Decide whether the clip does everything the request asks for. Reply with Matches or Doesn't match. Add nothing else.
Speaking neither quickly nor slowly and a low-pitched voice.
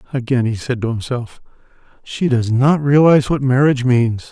Matches